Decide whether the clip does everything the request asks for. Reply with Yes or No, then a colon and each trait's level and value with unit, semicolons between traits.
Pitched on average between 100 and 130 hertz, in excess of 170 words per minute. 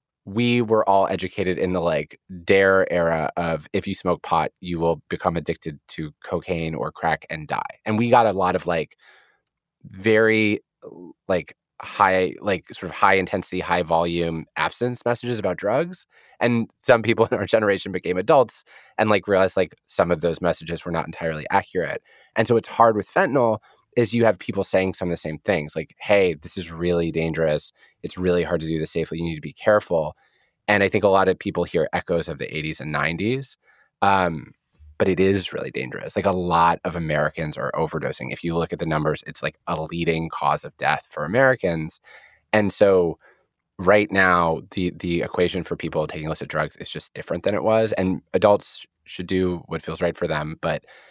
No: very low, 90 Hz; average, 200 wpm